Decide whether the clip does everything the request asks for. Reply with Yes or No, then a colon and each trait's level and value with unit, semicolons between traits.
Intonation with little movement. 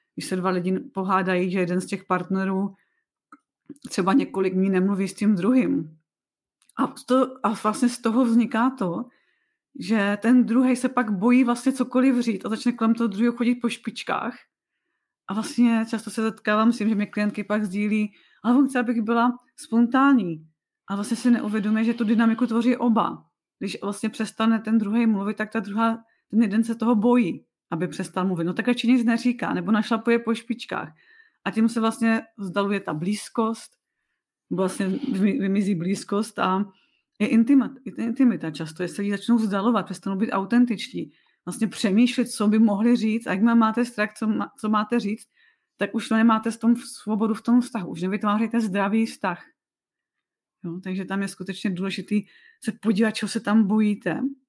No: average, 3.1 semitones